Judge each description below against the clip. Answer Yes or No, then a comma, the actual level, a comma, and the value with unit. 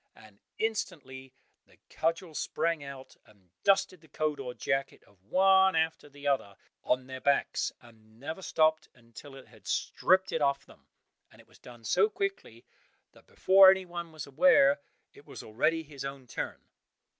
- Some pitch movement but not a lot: No, wide, 6.0 semitones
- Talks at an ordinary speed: Yes, average, 165 wpm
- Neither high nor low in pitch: Yes, medium, 145 Hz